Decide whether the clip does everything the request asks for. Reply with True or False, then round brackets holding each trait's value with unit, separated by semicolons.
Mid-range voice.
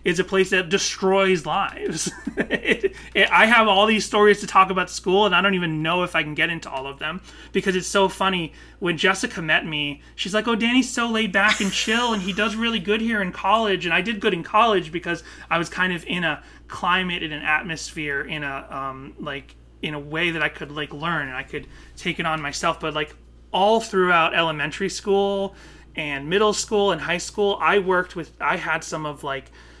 True (180 Hz)